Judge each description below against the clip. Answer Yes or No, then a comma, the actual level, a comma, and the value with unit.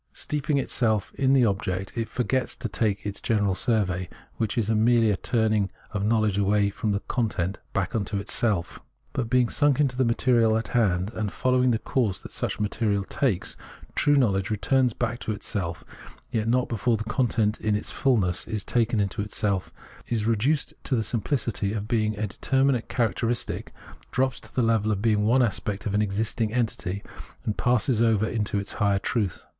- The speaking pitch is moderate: No, low, 110 Hz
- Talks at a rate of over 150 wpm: Yes, average, 185 wpm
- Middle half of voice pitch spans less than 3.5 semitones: Yes, average, 3.0 semitones